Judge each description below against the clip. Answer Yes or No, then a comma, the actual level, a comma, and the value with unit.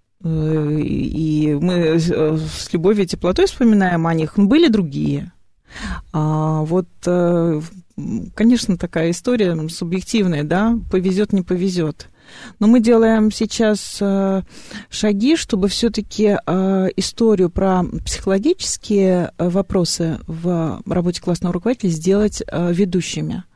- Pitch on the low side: No, medium, 185 Hz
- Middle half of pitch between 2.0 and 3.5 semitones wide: No, average, 3.9 semitones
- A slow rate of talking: Yes, slow, 95 wpm